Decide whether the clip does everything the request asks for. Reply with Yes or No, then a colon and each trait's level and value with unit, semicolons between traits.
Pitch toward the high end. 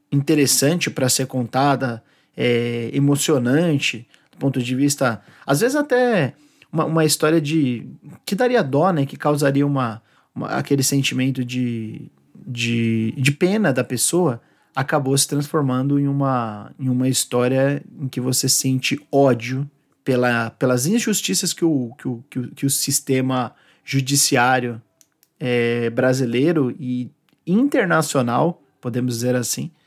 No: low, 135 Hz